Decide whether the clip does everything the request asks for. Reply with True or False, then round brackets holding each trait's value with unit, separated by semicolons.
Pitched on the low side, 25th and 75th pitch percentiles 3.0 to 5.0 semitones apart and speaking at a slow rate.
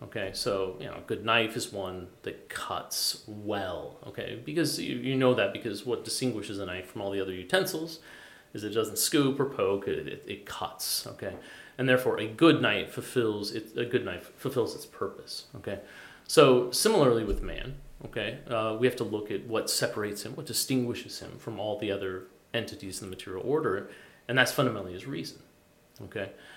False (115 Hz; 4.5 semitones; 190 wpm)